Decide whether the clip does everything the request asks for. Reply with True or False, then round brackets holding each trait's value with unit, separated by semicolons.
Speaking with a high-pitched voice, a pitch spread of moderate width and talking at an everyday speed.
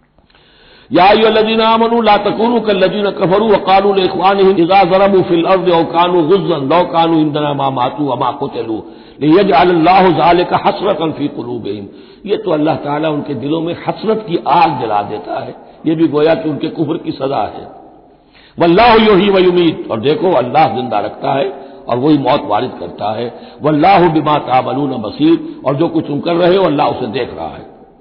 False (170 Hz; 4.5 semitones; 145 wpm)